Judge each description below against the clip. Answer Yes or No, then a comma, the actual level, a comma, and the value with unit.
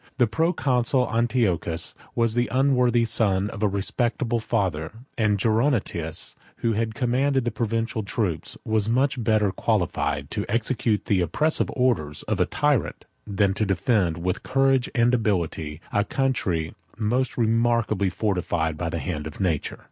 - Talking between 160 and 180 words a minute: No, average, 140 wpm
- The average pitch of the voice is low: Yes, low, 110 Hz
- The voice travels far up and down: No, average, 4.8 semitones